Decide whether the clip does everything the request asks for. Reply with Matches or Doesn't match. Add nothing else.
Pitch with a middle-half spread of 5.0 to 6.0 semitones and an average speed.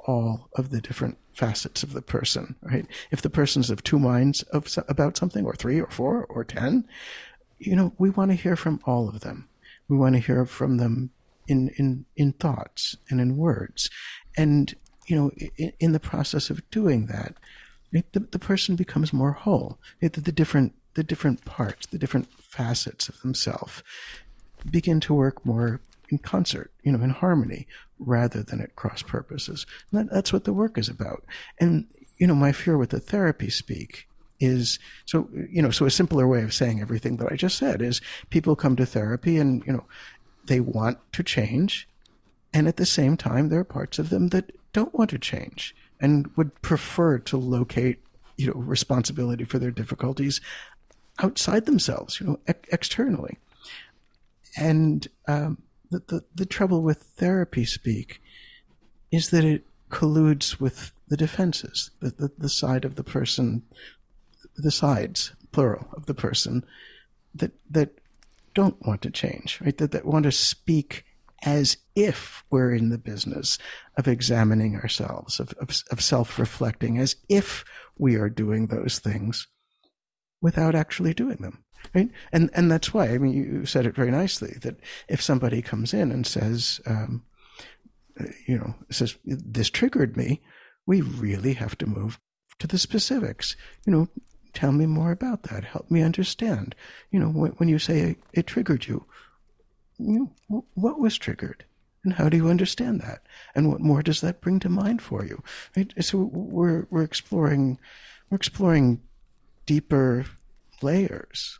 Matches